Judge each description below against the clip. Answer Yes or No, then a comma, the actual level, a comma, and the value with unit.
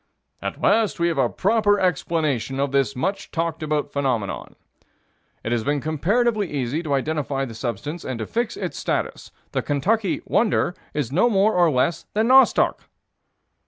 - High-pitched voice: No, medium, 155 Hz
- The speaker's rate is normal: Yes, average, 160 wpm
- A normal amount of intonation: No, wide, 6.6 semitones